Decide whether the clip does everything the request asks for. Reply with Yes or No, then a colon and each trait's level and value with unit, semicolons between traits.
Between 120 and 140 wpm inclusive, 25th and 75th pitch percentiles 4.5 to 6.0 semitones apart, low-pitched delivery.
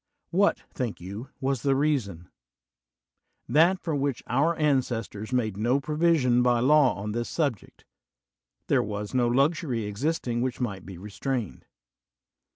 Yes: slow, 135 wpm; average, 5.1 semitones; low, 125 Hz